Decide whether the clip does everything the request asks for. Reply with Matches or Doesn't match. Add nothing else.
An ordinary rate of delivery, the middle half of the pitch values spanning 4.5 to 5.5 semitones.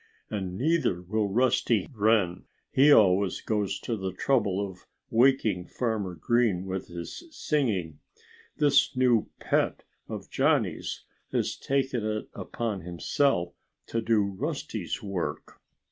Doesn't match